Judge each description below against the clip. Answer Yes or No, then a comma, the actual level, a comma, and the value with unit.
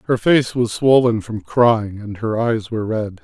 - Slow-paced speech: No, fast, 205 wpm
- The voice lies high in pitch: No, low, 115 Hz